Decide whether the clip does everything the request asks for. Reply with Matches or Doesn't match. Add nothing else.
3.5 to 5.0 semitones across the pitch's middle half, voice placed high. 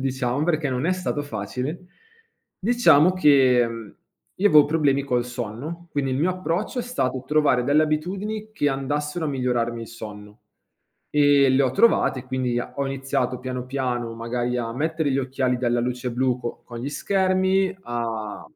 Doesn't match